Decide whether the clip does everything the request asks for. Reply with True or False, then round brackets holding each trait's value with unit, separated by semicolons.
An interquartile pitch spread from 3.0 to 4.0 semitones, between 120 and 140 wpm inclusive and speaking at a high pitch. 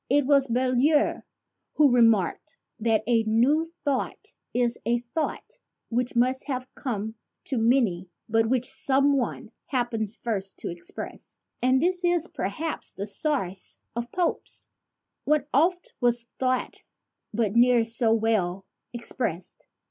True (3.6 semitones; 135 wpm; 245 Hz)